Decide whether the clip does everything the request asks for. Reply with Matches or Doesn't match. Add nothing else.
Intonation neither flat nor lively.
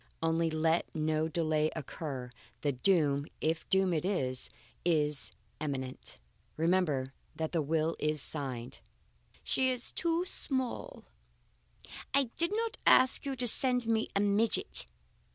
Doesn't match